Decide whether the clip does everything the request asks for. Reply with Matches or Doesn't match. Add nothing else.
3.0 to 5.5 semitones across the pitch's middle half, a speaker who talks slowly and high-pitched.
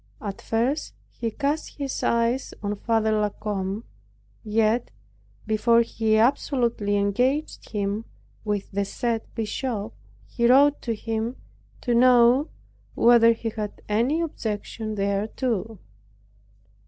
Doesn't match